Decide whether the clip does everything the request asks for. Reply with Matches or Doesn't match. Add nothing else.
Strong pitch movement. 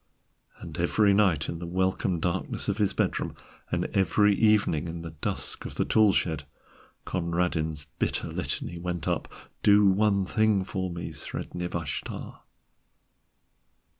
Doesn't match